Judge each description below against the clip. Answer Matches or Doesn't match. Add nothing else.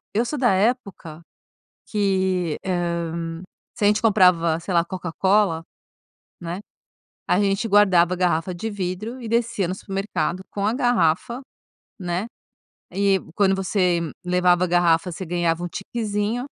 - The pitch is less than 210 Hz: Matches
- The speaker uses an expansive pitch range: Doesn't match